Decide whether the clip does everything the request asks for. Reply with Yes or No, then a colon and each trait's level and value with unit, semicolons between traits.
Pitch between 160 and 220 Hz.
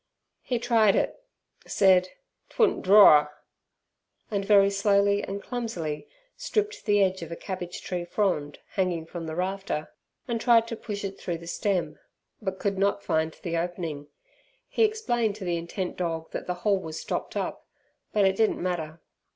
Yes: high, 190 Hz